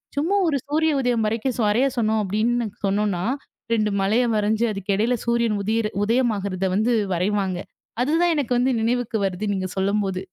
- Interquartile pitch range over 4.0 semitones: No, average, 3.4 semitones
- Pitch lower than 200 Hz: No, high, 220 Hz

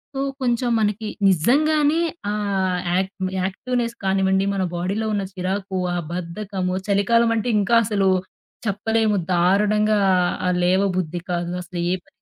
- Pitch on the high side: Yes, high, 200 Hz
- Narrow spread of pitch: No, average, 3.2 semitones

